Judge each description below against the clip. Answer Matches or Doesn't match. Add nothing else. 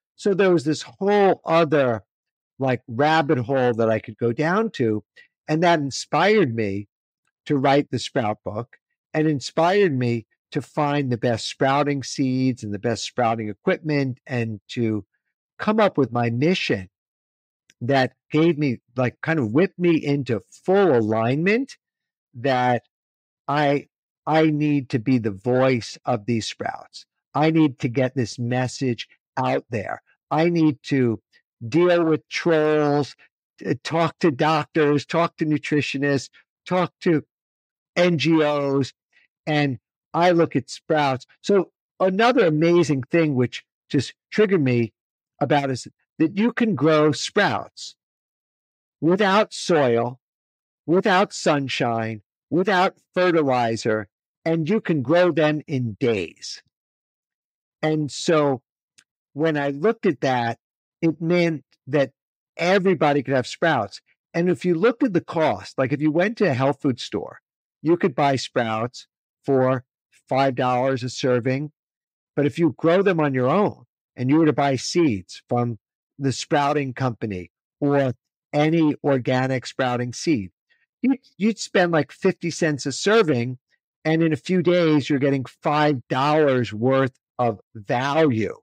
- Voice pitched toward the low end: Doesn't match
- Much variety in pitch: Doesn't match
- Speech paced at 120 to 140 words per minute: Matches